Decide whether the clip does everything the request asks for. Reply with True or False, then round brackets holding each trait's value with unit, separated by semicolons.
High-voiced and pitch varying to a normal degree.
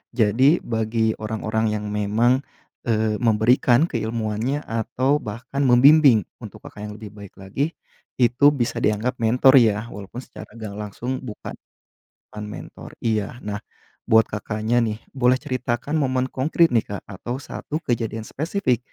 False (115 Hz; 3.2 semitones)